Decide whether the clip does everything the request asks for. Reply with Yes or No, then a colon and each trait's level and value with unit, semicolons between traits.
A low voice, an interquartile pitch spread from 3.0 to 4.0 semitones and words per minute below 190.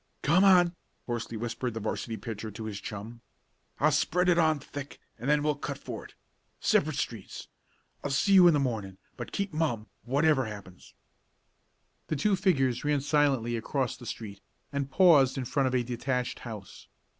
No: low, 130 Hz; average, 4.7 semitones; average, 175 wpm